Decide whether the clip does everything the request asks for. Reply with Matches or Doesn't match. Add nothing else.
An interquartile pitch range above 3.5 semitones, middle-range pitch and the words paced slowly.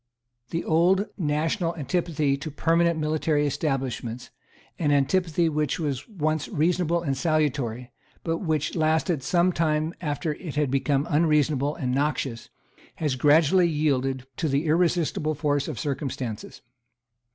Doesn't match